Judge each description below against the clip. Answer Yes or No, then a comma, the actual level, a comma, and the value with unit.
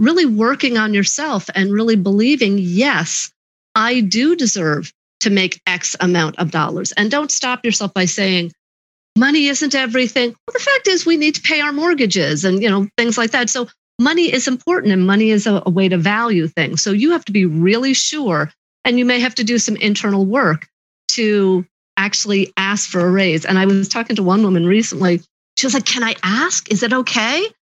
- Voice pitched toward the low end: No, high, 220 Hz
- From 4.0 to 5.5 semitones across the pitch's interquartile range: Yes, average, 5.0 semitones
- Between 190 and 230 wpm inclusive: Yes, average, 200 wpm